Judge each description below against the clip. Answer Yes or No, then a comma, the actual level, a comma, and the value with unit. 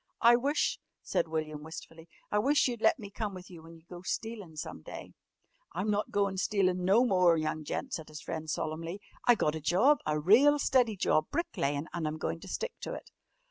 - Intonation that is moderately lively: No, wide, 5.9 semitones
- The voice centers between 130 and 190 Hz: Yes, medium, 185 Hz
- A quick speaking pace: Yes, fast, 215 wpm